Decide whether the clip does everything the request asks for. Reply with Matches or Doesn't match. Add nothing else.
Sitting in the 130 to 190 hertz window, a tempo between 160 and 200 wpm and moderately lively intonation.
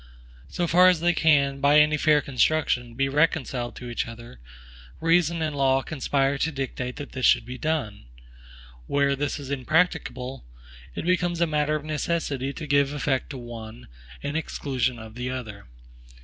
Matches